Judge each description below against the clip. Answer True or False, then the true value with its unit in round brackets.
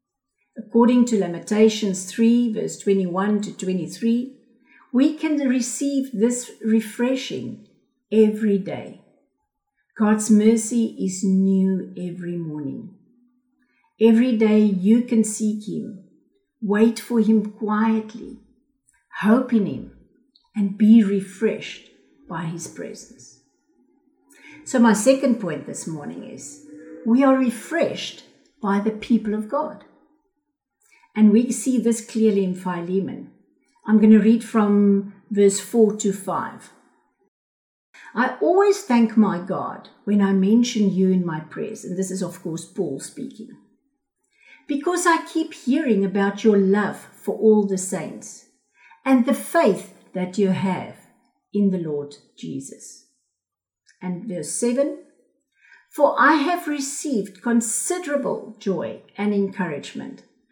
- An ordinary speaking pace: False (120 wpm)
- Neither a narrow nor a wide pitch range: True (4.7 semitones)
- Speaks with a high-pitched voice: True (220 Hz)